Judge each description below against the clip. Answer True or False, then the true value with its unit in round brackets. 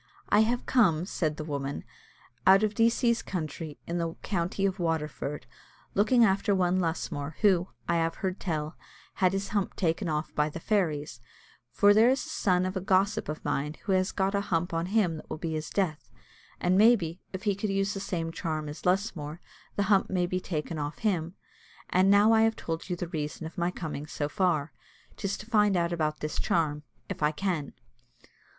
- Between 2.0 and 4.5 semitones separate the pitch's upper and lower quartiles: True (4.0 semitones)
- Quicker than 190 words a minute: True (200 wpm)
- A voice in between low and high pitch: True (180 Hz)